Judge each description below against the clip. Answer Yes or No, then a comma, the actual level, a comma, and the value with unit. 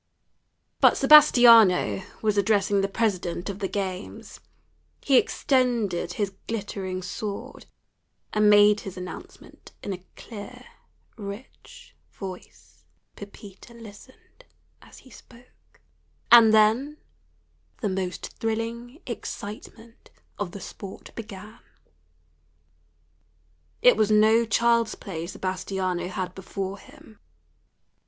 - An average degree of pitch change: Yes, average, 3.1 semitones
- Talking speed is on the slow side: Yes, slow, 100 wpm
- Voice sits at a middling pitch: No, high, 205 Hz